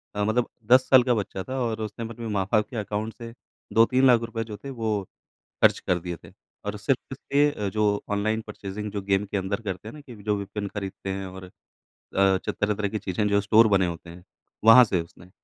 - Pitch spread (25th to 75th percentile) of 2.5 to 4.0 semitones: Yes, average, 2.8 semitones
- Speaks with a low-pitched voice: Yes, low, 105 Hz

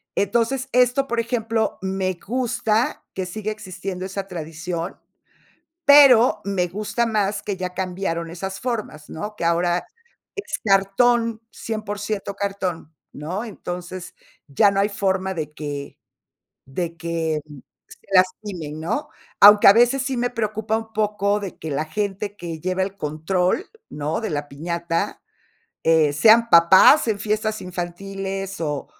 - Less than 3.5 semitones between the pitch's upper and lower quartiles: No, average, 4.1 semitones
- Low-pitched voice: No, high, 195 Hz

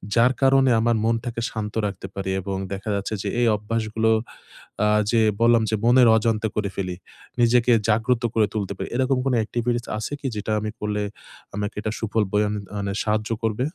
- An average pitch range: No, narrow, 2.2 semitones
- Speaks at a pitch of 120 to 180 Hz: No, low, 110 Hz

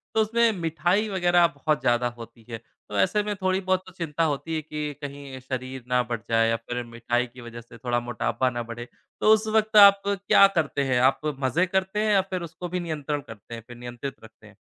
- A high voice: No, medium, 140 Hz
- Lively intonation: Yes, wide, 7.3 semitones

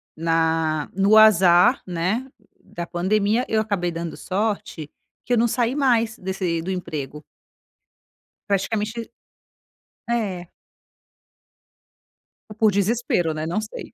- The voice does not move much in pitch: No, average, 4.4 semitones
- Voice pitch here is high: Yes, high, 195 Hz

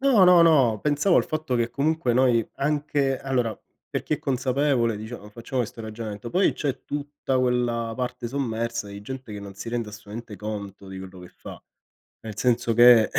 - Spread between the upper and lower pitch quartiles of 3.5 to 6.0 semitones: Yes, average, 4.0 semitones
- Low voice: Yes, low, 120 Hz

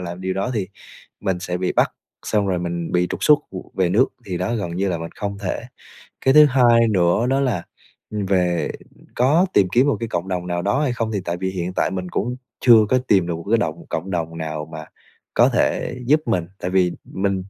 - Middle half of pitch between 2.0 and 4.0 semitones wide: No, average, 4.7 semitones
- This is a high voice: No, very low, 95 Hz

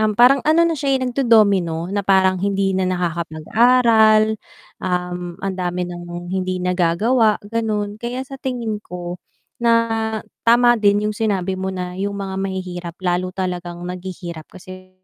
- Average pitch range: Yes, average, 3.7 semitones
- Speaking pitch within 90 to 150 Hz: No, high, 190 Hz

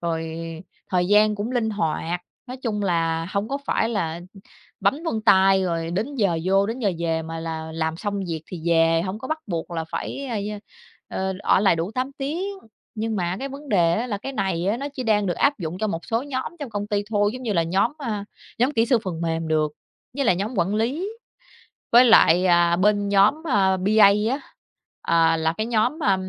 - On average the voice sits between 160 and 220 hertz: Yes, high, 200 Hz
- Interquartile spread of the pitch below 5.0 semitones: No, average, 5.3 semitones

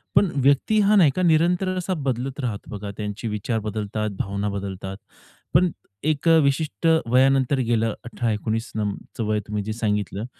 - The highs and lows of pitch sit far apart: Yes, wide, 5.8 semitones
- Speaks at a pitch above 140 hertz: No, low, 115 Hz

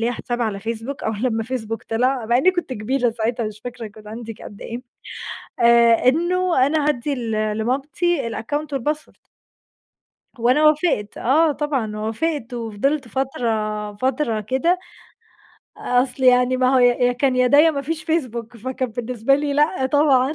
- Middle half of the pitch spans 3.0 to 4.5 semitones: Yes, average, 4.0 semitones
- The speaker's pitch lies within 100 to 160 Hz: No, very high, 250 Hz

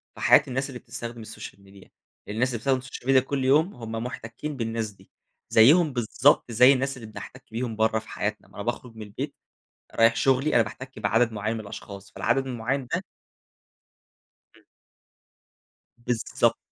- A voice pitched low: Yes, low, 120 Hz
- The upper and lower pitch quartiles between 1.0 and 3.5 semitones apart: Yes, average, 3.1 semitones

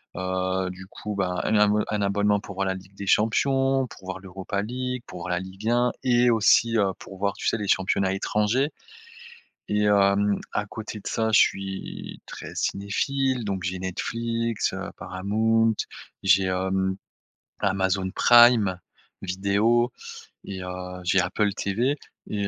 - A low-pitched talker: Yes, low, 100 Hz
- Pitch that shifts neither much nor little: Yes, average, 3.0 semitones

